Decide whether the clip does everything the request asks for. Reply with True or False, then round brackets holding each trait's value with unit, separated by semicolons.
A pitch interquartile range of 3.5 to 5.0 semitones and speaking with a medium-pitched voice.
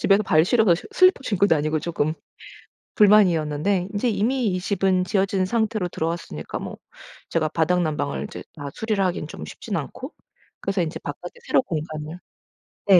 True (4.4 semitones; 180 Hz)